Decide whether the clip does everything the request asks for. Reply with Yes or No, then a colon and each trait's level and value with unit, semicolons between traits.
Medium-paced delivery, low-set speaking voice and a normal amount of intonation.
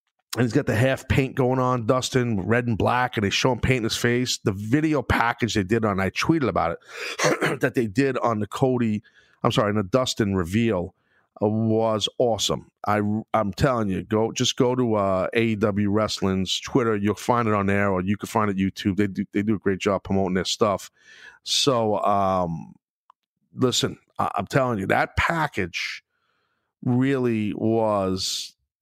Yes: average, 180 wpm; low, 110 Hz; average, 3.6 semitones